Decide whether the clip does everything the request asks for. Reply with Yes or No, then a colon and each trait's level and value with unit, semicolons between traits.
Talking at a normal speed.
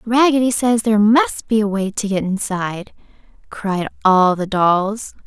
Yes: average, 160 wpm